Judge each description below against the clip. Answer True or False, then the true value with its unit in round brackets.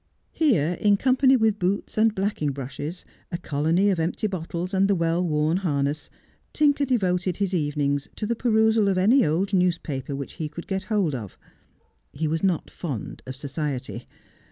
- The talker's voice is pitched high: False (180 Hz)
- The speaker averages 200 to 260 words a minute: False (170 wpm)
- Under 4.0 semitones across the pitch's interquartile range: False (5.2 semitones)